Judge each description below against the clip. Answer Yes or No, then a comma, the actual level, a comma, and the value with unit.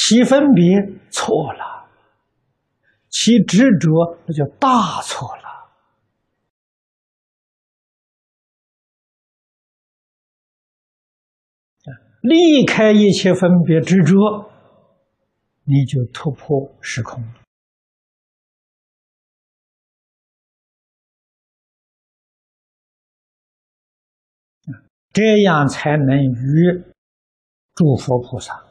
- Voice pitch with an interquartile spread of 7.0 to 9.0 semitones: Yes, wide, 7.5 semitones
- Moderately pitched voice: Yes, medium, 170 Hz